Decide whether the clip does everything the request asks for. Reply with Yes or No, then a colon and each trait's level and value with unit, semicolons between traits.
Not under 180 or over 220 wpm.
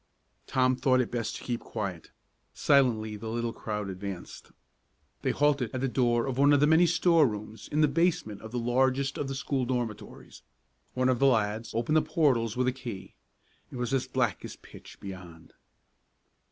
Yes: average, 185 wpm